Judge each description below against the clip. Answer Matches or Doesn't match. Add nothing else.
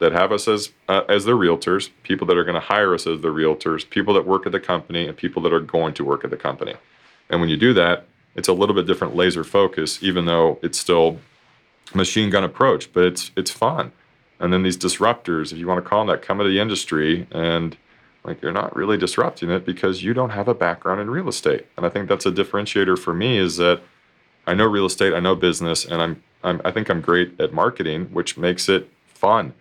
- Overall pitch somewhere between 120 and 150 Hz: Doesn't match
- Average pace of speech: Doesn't match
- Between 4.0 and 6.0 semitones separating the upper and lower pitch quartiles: Doesn't match